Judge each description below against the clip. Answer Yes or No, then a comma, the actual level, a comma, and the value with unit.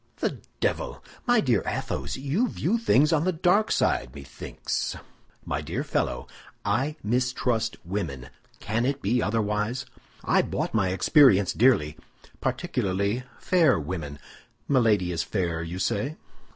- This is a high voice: No, low, 115 Hz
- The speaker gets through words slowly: Yes, slow, 125 wpm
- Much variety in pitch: Yes, wide, 7.3 semitones